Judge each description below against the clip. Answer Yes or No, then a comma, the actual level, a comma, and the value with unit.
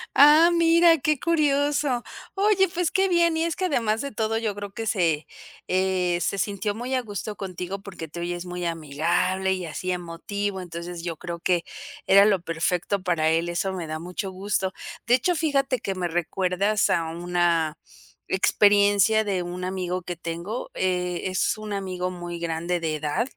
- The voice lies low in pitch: No, high, 190 Hz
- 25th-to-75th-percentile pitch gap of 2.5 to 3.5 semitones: No, average, 4.3 semitones